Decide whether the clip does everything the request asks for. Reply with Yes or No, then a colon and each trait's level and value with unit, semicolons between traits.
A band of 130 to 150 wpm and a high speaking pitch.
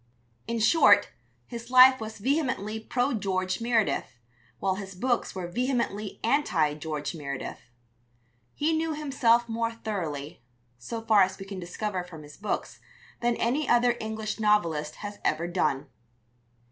Yes: average, 140 wpm; high, 215 Hz